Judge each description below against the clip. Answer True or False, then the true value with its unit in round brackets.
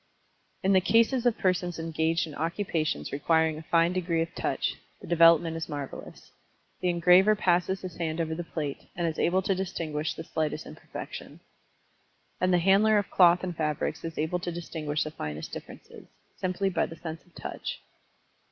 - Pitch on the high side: False (170 Hz)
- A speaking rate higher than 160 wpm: True (175 wpm)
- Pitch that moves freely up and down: False (2.5 semitones)